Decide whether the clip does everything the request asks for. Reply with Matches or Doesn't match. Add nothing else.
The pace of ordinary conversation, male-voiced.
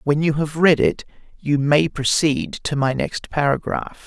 Matches